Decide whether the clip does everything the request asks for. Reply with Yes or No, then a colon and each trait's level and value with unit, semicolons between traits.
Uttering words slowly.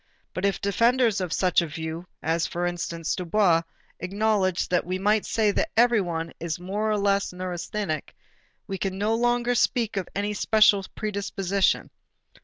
No: average, 155 wpm